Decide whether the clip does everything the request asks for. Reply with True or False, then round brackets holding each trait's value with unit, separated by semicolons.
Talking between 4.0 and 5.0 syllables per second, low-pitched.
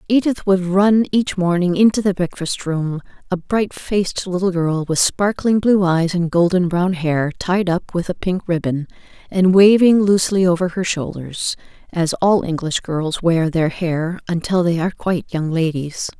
False (4.5 syllables/s; 180 Hz)